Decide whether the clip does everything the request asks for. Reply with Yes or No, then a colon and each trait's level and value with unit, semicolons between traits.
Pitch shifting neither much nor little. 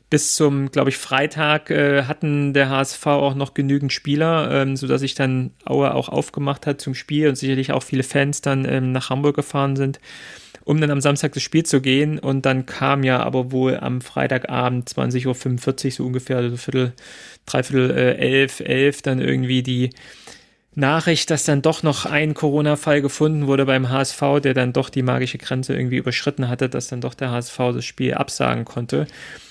No: narrow, 2.0 semitones